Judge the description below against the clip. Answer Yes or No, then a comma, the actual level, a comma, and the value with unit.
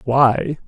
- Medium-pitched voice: No, low, 130 Hz